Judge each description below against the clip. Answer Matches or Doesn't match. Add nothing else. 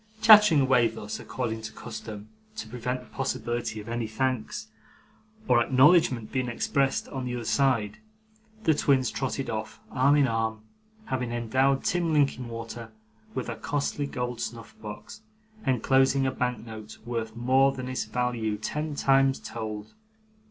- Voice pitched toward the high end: Doesn't match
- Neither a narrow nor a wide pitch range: Matches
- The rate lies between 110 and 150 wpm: Matches